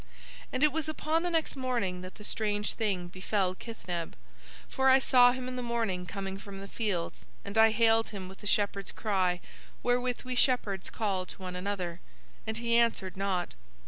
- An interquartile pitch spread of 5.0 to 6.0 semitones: No, average, 4.6 semitones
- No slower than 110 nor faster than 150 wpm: No, average, 185 wpm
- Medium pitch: No, high, 210 Hz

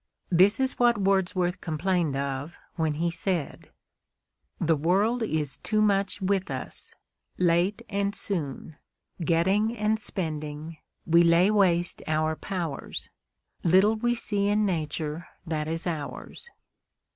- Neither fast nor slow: No, slow, 120 wpm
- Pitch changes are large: No, average, 4.2 semitones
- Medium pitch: Yes, medium, 175 Hz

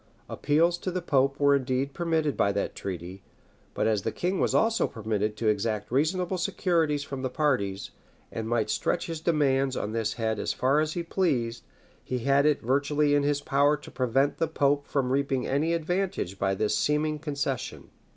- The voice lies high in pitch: No, medium, 140 Hz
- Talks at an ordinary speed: Yes, average, 185 wpm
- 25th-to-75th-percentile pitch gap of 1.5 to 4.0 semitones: No, average, 5.1 semitones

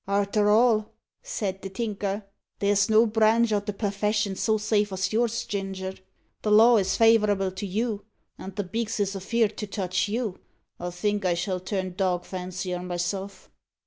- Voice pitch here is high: Yes, high, 205 Hz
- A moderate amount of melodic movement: No, narrow, 2.3 semitones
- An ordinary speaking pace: Yes, average, 165 wpm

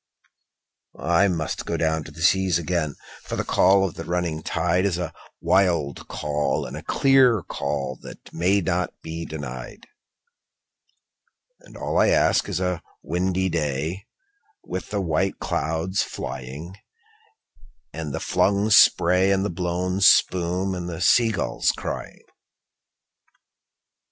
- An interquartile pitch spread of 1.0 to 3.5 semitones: Yes, average, 3.0 semitones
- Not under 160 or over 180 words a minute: No, slow, 135 wpm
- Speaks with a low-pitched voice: Yes, very low, 90 Hz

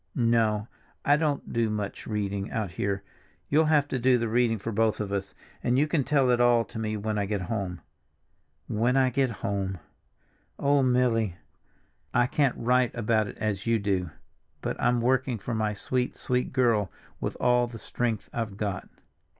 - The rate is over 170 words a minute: Yes, average, 180 wpm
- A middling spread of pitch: Yes, average, 3.2 semitones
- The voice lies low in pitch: Yes, low, 115 Hz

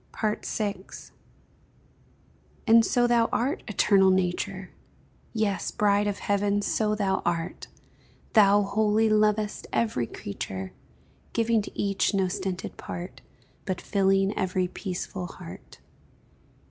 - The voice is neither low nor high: No, high, 200 Hz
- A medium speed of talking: No, slow, 110 wpm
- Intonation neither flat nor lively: No, narrow, 2.2 semitones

